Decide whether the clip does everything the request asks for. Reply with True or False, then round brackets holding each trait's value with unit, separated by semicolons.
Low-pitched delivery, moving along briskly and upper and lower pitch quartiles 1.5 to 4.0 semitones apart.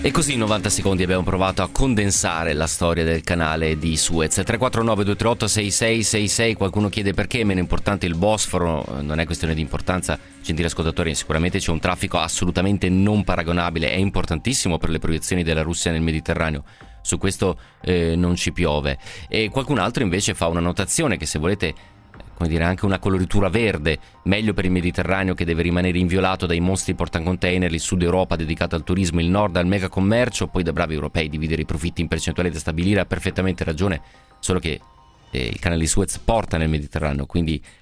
True (90 Hz; 185 wpm; 3.2 semitones)